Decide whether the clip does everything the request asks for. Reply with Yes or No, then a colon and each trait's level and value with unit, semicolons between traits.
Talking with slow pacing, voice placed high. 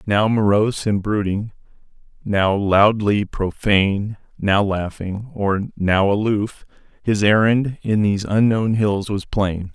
No: slow, 125 wpm; low, 105 Hz